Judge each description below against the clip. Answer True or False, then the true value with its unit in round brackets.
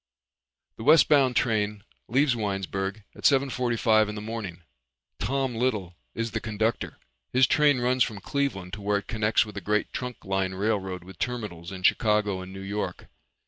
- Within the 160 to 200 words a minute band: True (170 wpm)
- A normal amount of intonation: True (4.2 semitones)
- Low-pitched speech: True (105 Hz)